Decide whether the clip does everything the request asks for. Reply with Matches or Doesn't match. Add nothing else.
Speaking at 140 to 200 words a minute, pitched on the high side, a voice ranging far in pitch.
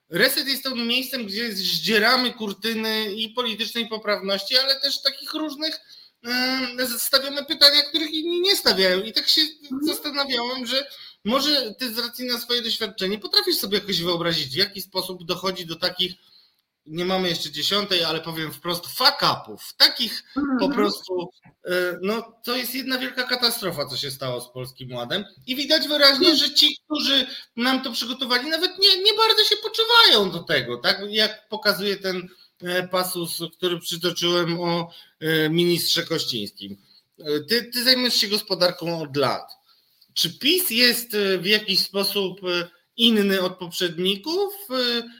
Matches